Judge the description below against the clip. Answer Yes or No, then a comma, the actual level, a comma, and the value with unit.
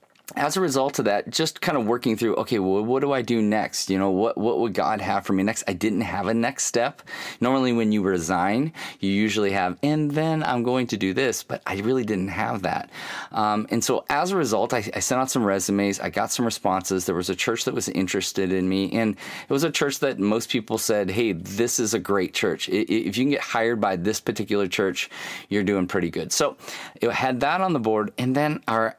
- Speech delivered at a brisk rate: Yes, fast, 240 wpm